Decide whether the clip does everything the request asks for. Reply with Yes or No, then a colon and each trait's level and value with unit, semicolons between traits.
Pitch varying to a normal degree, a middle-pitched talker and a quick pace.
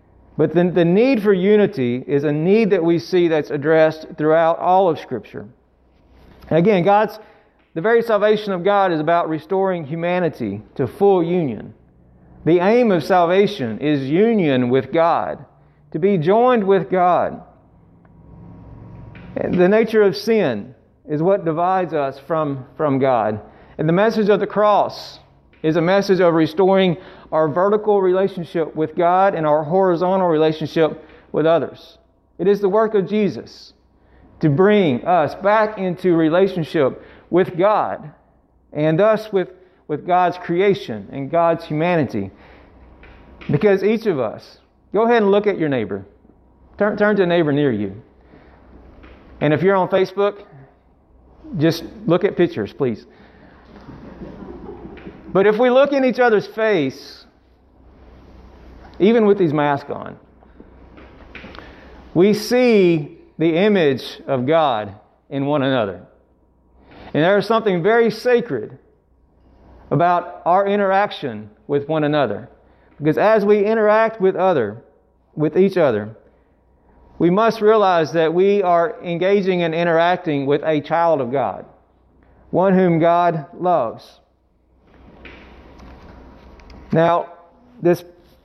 No: wide, 6.5 semitones; medium, 170 Hz; fast, 130 wpm